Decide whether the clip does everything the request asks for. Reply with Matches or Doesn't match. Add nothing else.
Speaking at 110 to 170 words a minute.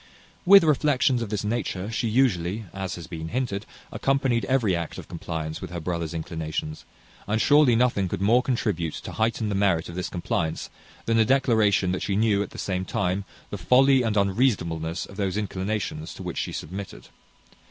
Doesn't match